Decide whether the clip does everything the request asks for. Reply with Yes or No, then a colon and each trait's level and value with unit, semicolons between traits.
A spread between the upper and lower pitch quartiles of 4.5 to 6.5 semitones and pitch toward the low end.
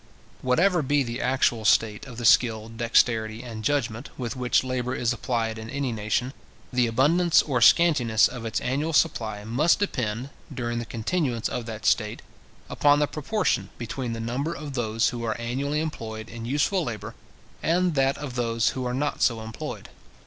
No: average, 3.8 semitones; low, 125 Hz